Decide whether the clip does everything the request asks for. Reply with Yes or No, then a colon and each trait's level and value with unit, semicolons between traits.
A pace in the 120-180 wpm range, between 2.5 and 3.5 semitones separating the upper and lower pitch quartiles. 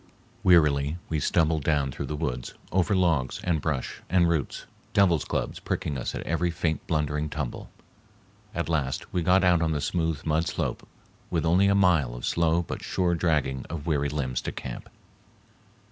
Yes: average, 175 wpm; average, 2.9 semitones